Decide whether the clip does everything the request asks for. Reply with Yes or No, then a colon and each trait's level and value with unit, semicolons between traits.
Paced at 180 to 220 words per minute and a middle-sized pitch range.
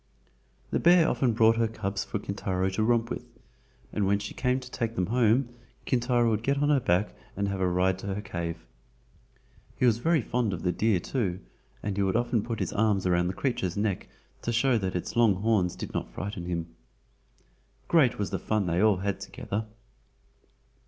Yes: average, 195 wpm; average, 4.0 semitones